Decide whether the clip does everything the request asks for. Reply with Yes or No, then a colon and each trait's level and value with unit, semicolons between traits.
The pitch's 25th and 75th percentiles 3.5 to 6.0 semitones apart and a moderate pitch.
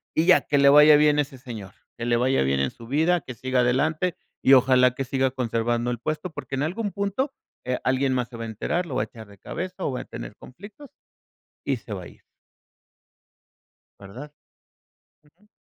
No: average, 4.7 semitones; low, 130 Hz